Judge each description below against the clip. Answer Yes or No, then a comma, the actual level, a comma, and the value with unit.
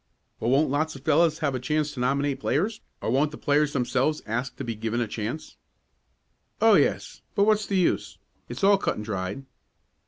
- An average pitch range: Yes, average, 4.1 semitones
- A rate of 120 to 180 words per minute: No, average, 195 wpm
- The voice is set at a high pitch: No, medium, 140 Hz